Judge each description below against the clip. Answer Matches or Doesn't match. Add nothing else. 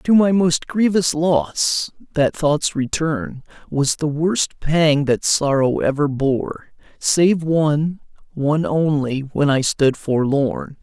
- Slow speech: Matches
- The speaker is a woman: Doesn't match